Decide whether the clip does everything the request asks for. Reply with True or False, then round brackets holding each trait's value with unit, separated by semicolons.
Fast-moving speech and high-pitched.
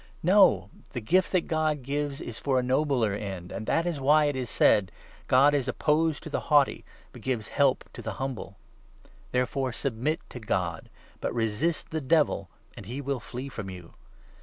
False (210 wpm; 130 Hz)